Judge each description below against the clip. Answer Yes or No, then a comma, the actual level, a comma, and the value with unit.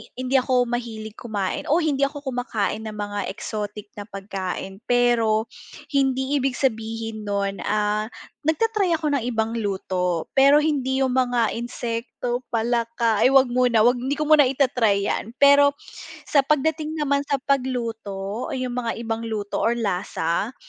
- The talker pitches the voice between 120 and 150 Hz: No, high, 240 Hz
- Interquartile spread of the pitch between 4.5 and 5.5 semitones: No, average, 3.8 semitones